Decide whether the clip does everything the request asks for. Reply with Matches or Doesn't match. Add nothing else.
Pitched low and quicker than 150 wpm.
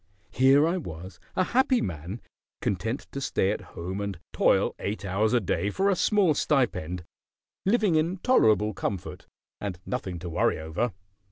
Matches